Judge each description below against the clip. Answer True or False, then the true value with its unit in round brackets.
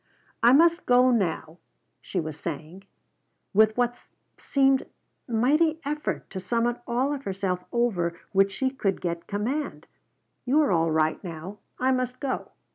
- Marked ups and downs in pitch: True (6.4 semitones)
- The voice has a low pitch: False (230 Hz)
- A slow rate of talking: False (145 wpm)